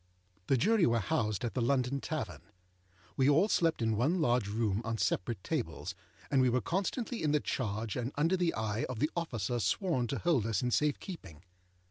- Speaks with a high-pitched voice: No, low, 125 Hz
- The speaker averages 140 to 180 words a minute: No, average, 195 wpm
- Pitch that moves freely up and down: Yes, wide, 6.0 semitones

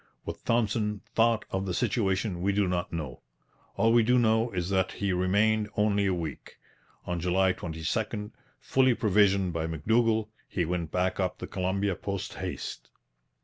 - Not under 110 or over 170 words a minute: Yes, average, 160 wpm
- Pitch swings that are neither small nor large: Yes, average, 3.4 semitones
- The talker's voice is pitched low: Yes, low, 100 Hz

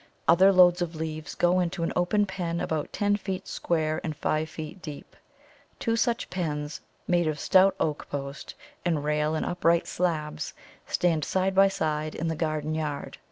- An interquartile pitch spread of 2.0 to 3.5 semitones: Yes, average, 3.0 semitones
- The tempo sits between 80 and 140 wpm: No, average, 170 wpm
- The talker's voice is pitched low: No, medium, 165 Hz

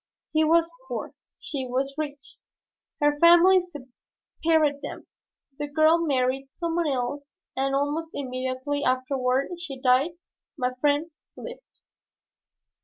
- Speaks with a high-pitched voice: Yes, very high, 285 Hz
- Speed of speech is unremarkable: No, slow, 115 wpm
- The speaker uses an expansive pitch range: No, average, 3.6 semitones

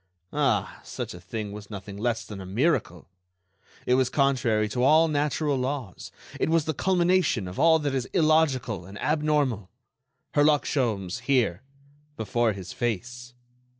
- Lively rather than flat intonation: Yes, wide, 5.8 semitones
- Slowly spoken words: No, average, 145 wpm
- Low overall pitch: Yes, low, 125 Hz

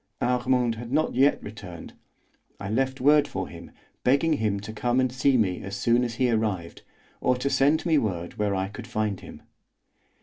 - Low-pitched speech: Yes, low, 120 Hz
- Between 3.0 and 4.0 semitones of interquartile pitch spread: No, average, 4.4 semitones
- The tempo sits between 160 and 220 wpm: Yes, average, 190 wpm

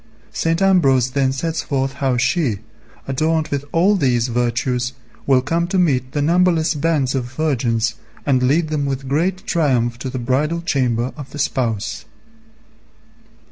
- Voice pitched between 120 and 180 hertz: Yes, low, 135 Hz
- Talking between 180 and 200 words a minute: No, average, 150 wpm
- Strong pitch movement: No, average, 4.3 semitones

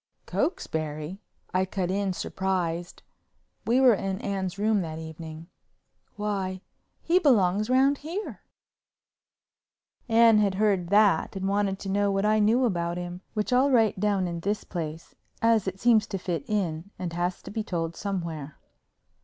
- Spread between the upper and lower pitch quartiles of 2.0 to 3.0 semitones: No, average, 3.4 semitones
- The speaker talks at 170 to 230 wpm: No, average, 145 wpm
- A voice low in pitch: No, high, 195 Hz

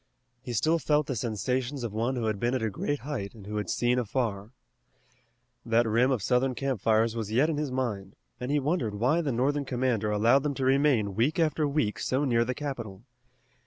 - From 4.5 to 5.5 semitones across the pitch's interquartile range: No, average, 4.0 semitones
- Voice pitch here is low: Yes, low, 125 Hz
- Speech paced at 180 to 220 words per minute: Yes, fast, 205 wpm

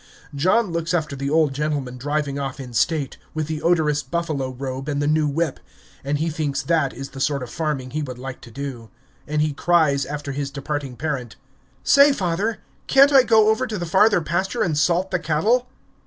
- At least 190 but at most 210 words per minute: Yes, average, 200 wpm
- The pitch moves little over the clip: No, average, 3.6 semitones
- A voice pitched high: No, medium, 150 Hz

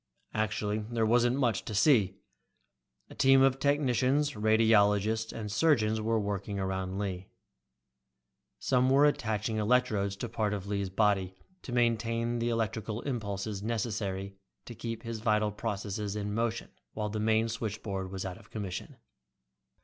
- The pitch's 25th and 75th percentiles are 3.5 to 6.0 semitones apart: No, narrow, 2.5 semitones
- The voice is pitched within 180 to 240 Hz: No, low, 110 Hz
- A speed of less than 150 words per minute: Yes, average, 140 wpm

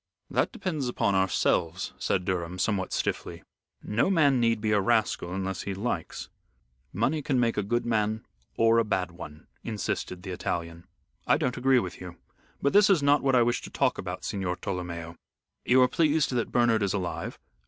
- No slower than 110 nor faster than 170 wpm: No, average, 185 wpm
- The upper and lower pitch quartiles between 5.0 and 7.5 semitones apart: Yes, average, 5.3 semitones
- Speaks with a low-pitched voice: Yes, low, 105 Hz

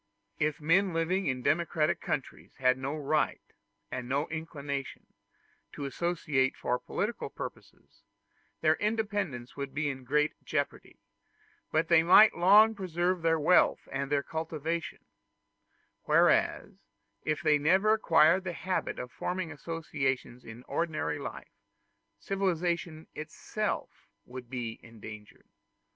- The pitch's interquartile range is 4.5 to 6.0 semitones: No, average, 4.1 semitones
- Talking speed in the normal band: No, slow, 120 wpm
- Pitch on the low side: No, medium, 155 Hz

